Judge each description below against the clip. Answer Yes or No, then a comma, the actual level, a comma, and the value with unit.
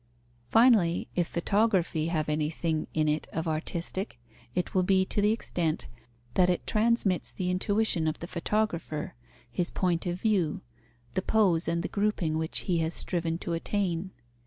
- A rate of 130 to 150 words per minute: No, average, 160 wpm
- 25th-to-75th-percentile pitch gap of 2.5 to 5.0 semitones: Yes, average, 3.4 semitones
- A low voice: No, medium, 175 Hz